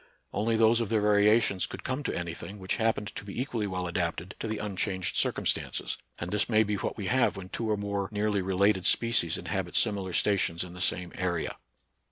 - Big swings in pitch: No, average, 2.9 semitones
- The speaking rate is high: Yes, fast, 220 wpm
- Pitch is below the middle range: Yes, low, 100 Hz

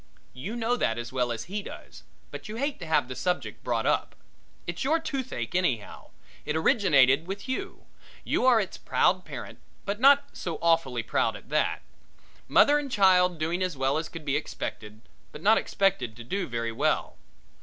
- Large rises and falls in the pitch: Yes, wide, 8.2 semitones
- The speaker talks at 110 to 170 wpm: No, average, 185 wpm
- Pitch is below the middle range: No, medium, 170 Hz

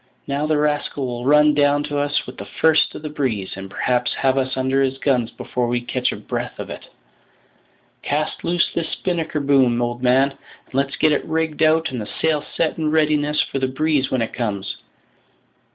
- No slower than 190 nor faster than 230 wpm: Yes, fast, 205 wpm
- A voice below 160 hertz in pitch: Yes, medium, 140 Hz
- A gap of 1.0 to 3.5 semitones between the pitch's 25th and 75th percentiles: Yes, average, 3.2 semitones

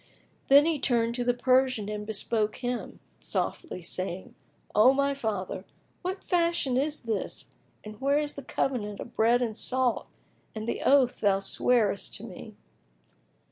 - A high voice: Yes, high, 245 Hz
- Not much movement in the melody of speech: No, average, 4.2 semitones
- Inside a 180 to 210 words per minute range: No, average, 150 wpm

